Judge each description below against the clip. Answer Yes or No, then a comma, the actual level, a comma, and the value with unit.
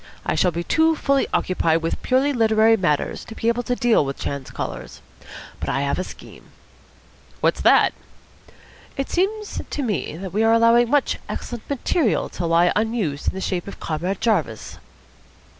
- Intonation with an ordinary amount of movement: No, wide, 6.2 semitones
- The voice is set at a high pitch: Yes, high, 220 Hz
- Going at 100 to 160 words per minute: No, average, 175 wpm